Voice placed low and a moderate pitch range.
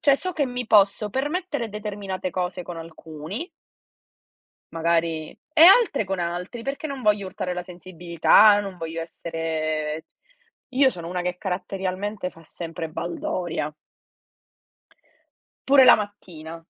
No: medium, 185 Hz; average, 4.7 semitones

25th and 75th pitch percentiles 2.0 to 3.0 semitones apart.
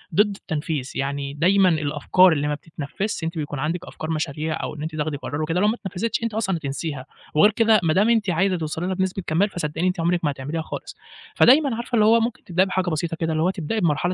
No: average, 4.2 semitones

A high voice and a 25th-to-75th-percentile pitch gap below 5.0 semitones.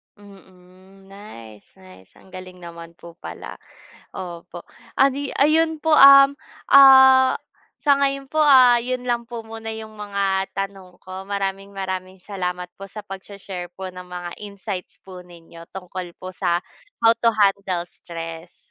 Yes: high, 195 Hz; average, 4.3 semitones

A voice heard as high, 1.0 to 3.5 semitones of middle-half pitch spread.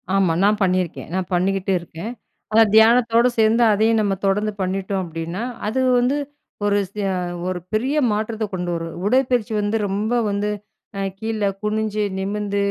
Yes: high, 205 Hz; narrow, 2.5 semitones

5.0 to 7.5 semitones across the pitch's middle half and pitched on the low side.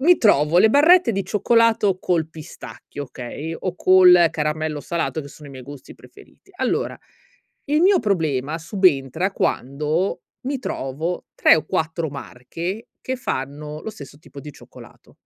No: wide, 5.4 semitones; medium, 165 Hz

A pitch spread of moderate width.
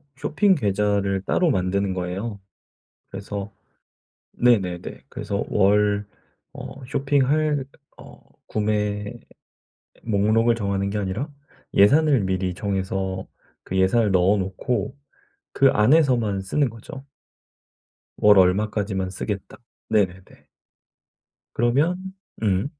Yes: average, 3.7 semitones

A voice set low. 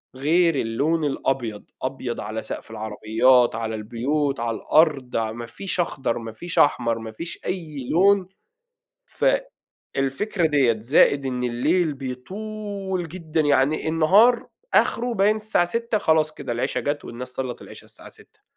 No: medium, 145 Hz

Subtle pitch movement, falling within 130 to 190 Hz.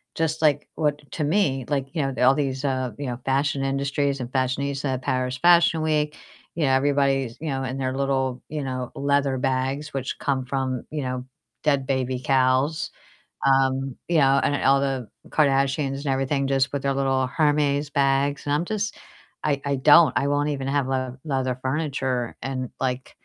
Yes: narrow, 1.6 semitones; low, 135 Hz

